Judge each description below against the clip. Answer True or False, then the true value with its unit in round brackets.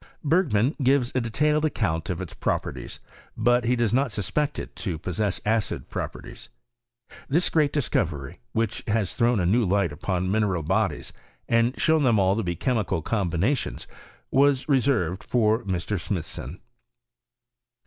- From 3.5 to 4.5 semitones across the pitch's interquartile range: False (5.6 semitones)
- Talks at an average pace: True (150 wpm)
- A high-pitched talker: False (110 Hz)